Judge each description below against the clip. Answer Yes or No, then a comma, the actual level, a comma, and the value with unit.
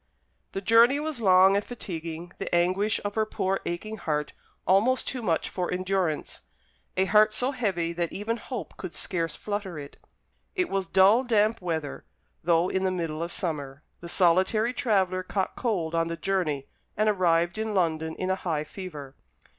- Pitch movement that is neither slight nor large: Yes, average, 4.2 semitones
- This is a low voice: No, medium, 185 Hz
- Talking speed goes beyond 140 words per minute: Yes, average, 170 wpm